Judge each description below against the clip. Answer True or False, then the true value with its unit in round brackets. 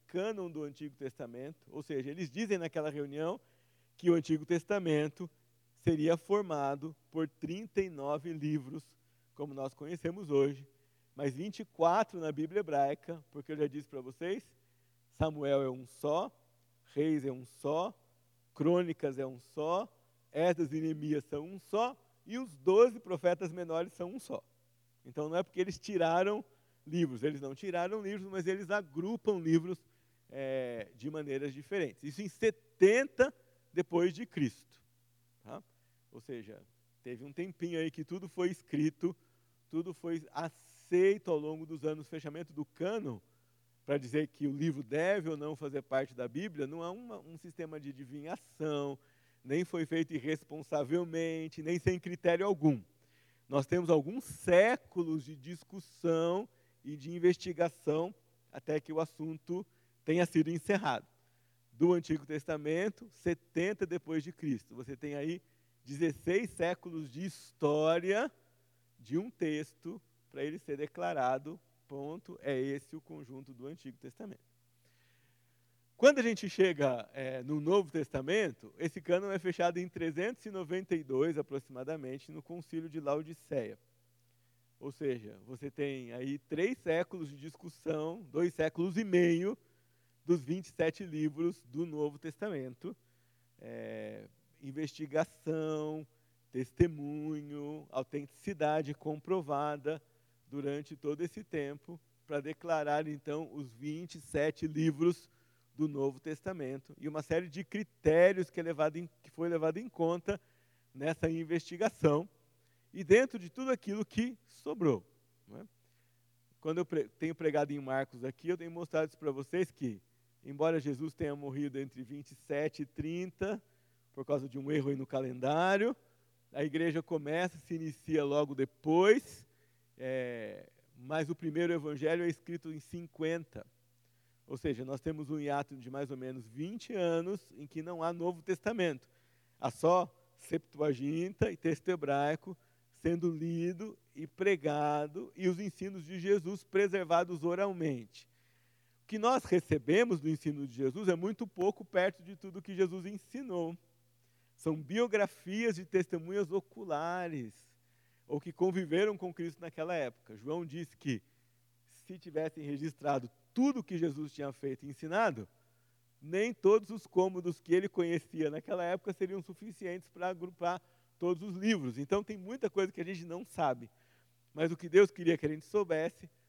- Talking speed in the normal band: True (140 wpm)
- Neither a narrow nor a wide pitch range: True (4.6 semitones)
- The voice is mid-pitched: True (155 Hz)